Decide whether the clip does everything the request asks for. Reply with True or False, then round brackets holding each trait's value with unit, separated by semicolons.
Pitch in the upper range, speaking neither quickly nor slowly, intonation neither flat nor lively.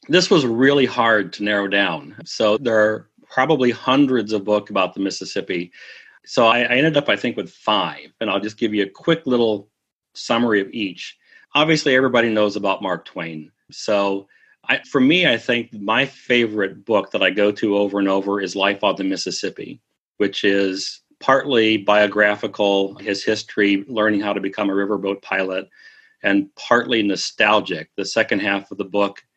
False (105 Hz; 175 wpm; 3.1 semitones)